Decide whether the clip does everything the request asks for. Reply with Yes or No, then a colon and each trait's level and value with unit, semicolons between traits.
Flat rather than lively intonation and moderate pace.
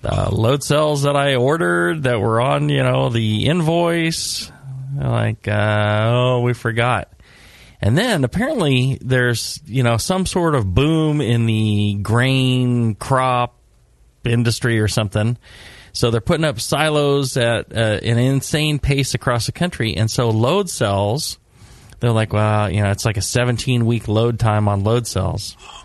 No: average, 3.8 semitones; average, 160 wpm